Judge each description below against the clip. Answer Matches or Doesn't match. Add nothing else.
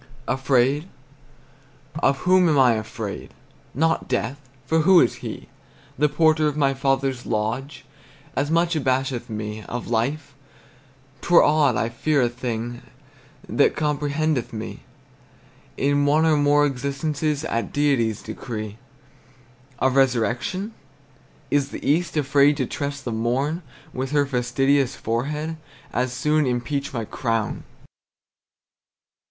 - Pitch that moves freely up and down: Doesn't match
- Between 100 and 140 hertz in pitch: Matches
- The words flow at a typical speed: Doesn't match